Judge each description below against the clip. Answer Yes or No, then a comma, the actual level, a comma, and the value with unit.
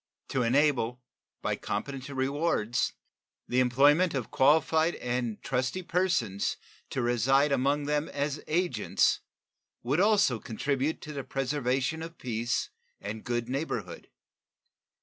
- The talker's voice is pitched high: No, low, 135 Hz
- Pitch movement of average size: Yes, average, 3.5 semitones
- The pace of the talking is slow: Yes, slow, 115 wpm